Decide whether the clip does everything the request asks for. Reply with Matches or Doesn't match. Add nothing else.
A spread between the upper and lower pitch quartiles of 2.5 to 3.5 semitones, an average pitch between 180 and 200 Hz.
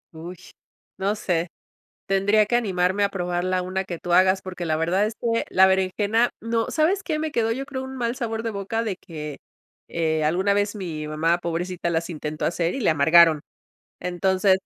Doesn't match